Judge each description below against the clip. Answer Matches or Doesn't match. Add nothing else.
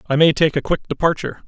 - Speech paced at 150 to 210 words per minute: Doesn't match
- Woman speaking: Doesn't match